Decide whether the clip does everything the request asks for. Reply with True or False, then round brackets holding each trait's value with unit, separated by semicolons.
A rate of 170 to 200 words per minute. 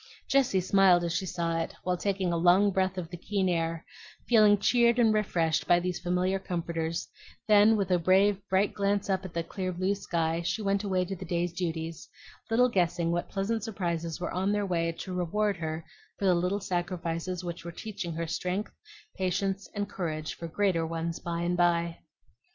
True (190 wpm)